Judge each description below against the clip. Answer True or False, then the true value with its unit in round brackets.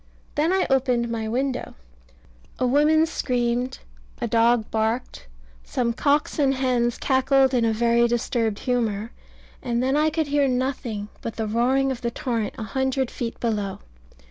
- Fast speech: False (155 wpm)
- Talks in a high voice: True (245 Hz)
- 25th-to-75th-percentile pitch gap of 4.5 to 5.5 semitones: False (2.6 semitones)